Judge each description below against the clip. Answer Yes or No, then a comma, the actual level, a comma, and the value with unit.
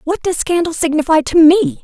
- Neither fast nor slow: Yes, average, 195 wpm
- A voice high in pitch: Yes, very high, 320 Hz